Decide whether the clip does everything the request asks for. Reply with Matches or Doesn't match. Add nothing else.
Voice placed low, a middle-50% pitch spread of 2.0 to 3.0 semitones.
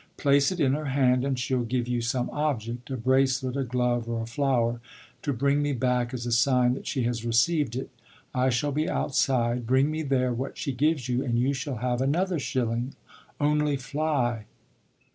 Matches